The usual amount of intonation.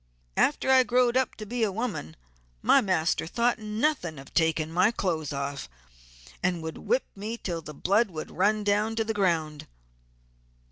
No: wide, 6.2 semitones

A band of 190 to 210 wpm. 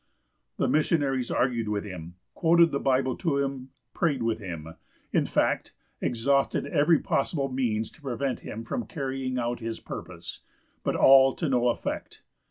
No: average, 150 wpm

